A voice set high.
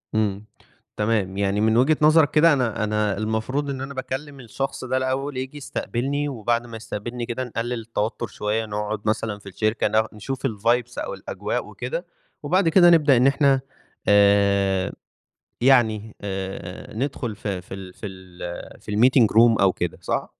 No: low, 115 Hz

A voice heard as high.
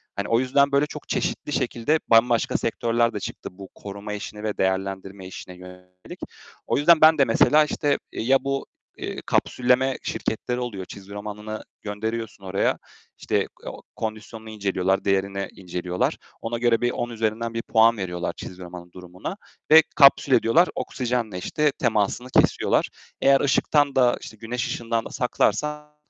No: low, 115 Hz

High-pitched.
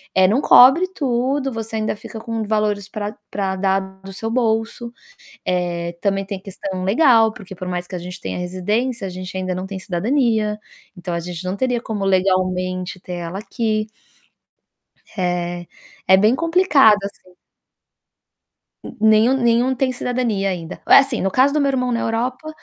Yes: high, 210 Hz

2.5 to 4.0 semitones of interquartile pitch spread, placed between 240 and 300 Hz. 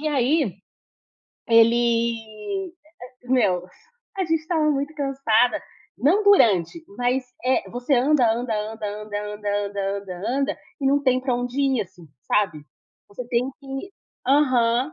No: average, 4.5 semitones; high, 245 Hz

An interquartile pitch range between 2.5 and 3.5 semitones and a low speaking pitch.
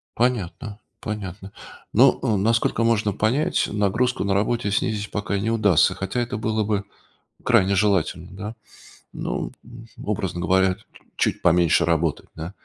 Yes: average, 3.1 semitones; low, 105 Hz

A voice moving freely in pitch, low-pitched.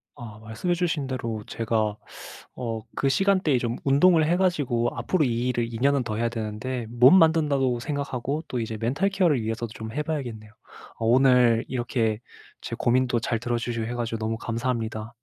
No: average, 3.7 semitones; low, 120 Hz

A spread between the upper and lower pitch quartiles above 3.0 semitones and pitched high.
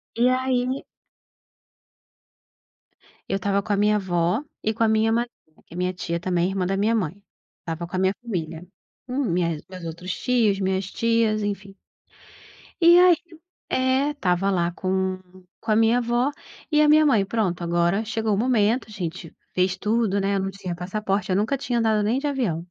Yes: average, 4.2 semitones; high, 200 Hz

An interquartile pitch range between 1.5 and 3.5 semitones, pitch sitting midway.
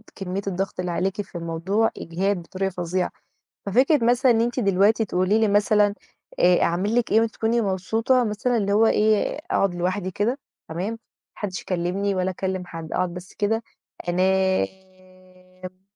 No: average, 2.9 semitones; high, 195 Hz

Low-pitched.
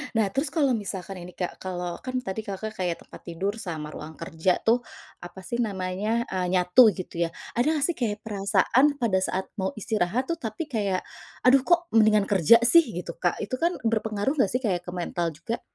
No: high, 205 Hz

